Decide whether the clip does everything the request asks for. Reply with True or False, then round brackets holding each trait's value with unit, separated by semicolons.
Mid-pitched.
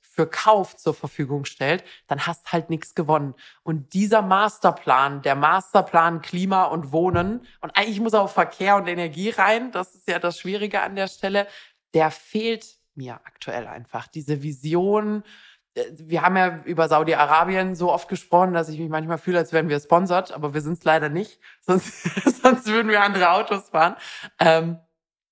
True (175 Hz)